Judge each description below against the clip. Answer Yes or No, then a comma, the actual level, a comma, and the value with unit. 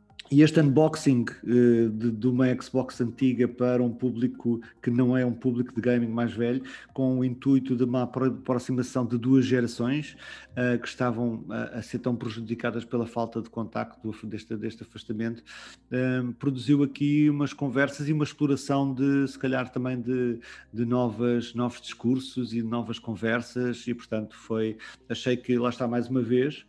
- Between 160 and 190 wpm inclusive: Yes, average, 165 wpm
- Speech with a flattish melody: Yes, narrow, 1.7 semitones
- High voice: No, low, 125 Hz